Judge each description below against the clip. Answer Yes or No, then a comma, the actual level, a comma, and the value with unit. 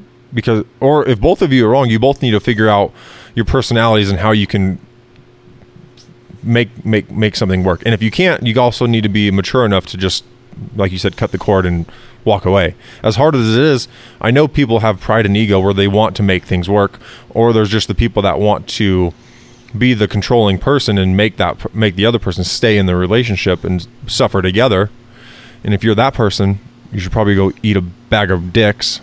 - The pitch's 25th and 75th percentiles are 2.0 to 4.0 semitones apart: Yes, average, 3.3 semitones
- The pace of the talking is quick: Yes, fast, 220 wpm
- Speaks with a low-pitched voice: Yes, low, 110 Hz